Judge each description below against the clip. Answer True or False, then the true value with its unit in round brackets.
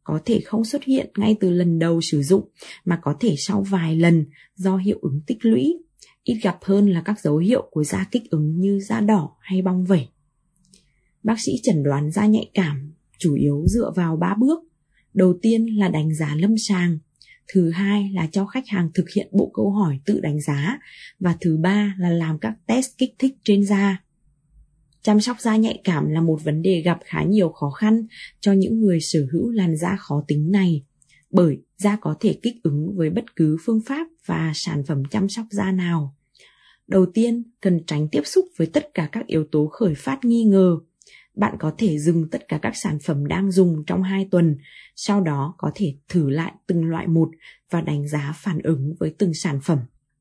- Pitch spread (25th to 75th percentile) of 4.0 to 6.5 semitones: True (4.7 semitones)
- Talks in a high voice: False (180 Hz)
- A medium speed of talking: True (210 wpm)